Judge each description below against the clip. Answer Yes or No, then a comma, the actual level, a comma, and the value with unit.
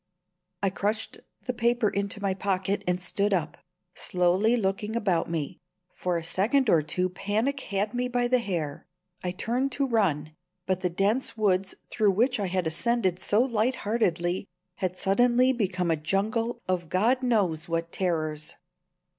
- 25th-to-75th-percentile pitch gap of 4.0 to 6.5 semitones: Yes, average, 4.6 semitones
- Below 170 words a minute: Yes, average, 160 wpm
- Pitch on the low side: No, high, 195 Hz